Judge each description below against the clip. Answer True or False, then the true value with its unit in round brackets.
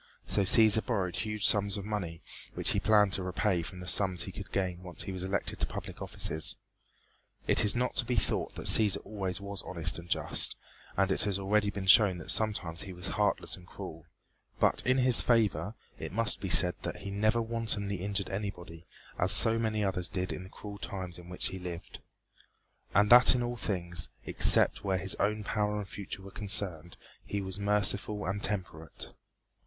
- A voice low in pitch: True (100 Hz)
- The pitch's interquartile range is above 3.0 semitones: False (2.5 semitones)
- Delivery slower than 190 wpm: False (200 wpm)